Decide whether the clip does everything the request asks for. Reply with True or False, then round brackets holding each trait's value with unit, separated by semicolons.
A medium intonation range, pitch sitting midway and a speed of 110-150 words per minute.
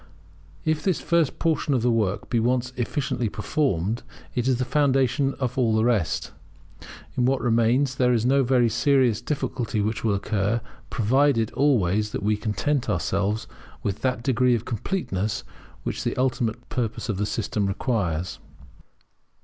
False (3.7 semitones; 120 Hz; 145 wpm)